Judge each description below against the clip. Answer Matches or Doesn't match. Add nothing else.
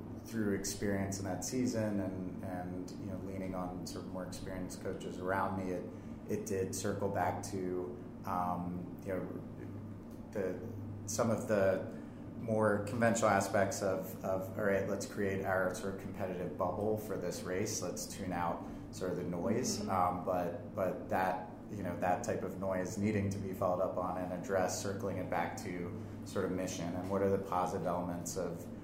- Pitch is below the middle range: Matches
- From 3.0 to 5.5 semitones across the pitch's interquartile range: Doesn't match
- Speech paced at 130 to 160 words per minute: Doesn't match